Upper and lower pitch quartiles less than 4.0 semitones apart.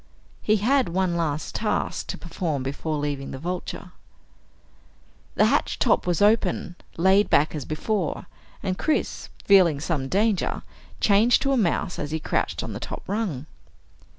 No: average, 5.0 semitones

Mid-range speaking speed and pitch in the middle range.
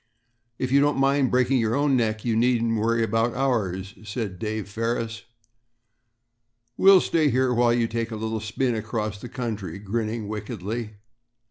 No: average, 150 wpm; low, 115 Hz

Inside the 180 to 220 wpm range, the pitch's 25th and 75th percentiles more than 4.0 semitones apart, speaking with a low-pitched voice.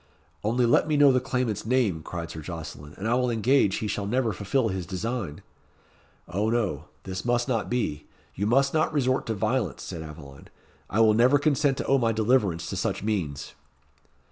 Yes: average, 190 wpm; wide, 5.6 semitones; low, 110 Hz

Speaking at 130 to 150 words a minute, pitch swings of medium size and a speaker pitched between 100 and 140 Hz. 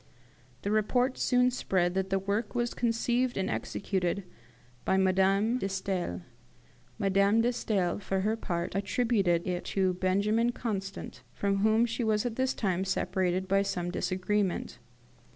No: average, 145 wpm; average, 3.2 semitones; high, 195 Hz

